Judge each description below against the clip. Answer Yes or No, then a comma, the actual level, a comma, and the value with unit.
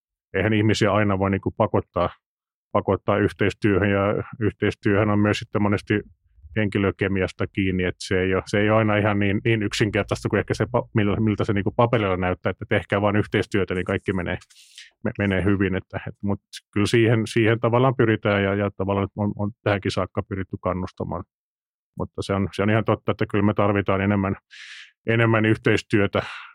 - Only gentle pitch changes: Yes, narrow, 1.9 semitones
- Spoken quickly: Yes, fast, 170 wpm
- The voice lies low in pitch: Yes, low, 105 Hz